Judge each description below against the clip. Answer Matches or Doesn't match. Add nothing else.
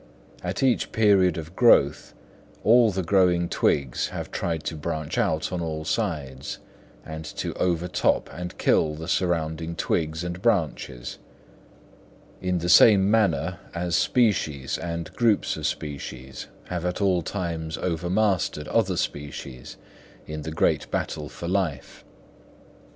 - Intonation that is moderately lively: Matches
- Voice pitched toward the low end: Matches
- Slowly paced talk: Matches